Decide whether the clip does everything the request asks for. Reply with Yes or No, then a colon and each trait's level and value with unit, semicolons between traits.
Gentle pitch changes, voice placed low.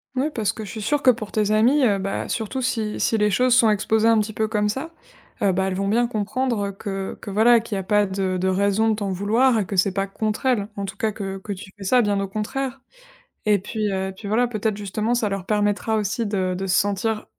No: narrow, 2.3 semitones; high, 210 Hz